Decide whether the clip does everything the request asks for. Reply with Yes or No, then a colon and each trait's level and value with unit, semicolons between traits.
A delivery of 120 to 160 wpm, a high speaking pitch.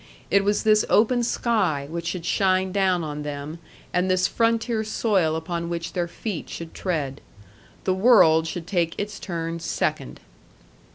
No: average, 155 wpm; medium, 180 Hz